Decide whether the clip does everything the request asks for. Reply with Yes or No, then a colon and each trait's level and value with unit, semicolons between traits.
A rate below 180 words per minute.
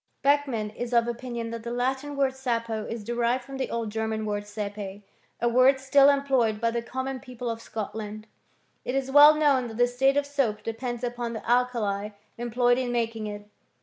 No: average, 200 wpm